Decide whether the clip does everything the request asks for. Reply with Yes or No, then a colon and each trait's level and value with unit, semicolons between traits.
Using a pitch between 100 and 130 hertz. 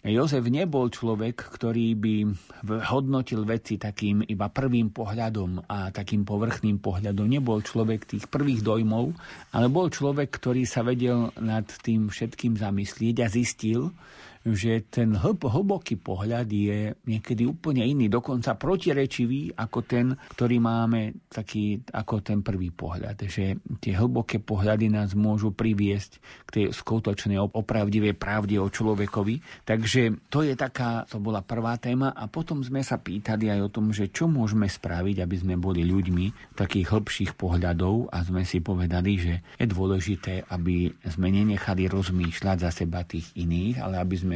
Yes: low, 110 Hz